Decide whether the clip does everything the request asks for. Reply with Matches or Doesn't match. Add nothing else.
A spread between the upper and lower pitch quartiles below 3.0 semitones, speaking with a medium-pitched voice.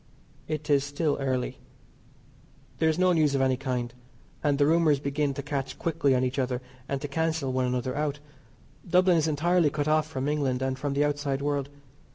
Matches